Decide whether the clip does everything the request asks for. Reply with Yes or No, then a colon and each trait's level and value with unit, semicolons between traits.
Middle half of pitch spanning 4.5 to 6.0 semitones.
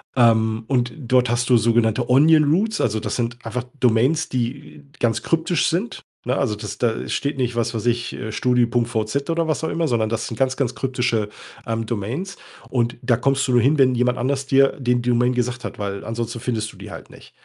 No: average, 2.8 semitones